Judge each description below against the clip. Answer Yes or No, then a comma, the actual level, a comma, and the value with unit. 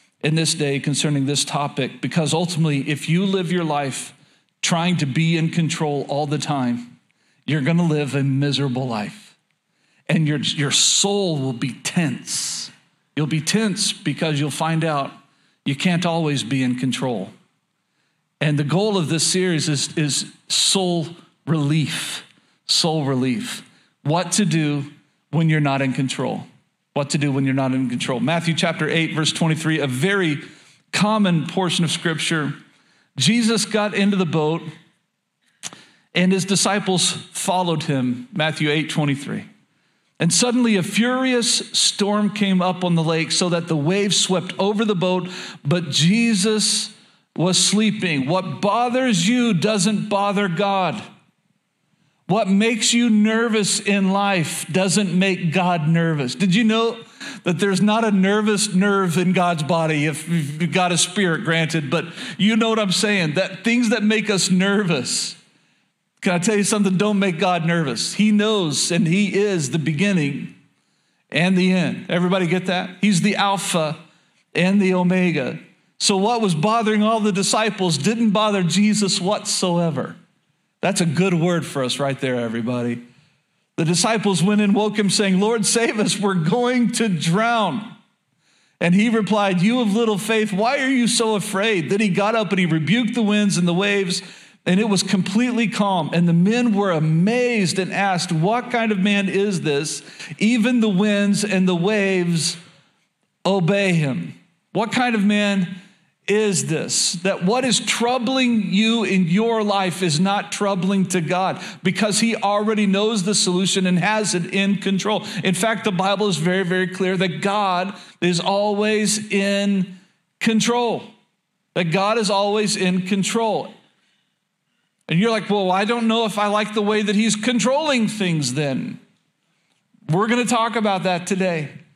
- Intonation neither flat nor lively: Yes, average, 4.1 semitones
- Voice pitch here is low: No, high, 190 Hz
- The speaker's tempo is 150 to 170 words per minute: Yes, average, 160 wpm